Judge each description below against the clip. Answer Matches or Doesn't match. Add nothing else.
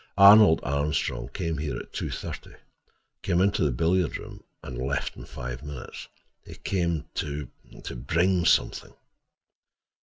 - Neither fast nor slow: Doesn't match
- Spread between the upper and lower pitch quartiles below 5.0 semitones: Matches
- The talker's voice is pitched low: Matches